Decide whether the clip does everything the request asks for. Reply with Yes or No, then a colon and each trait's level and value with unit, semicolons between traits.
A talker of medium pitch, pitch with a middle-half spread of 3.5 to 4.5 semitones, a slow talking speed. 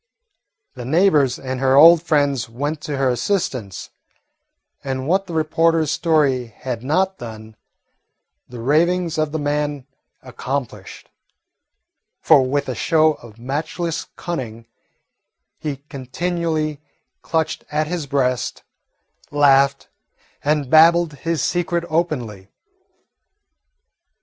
Yes: medium, 145 Hz; average, 4.1 semitones; slow, 105 wpm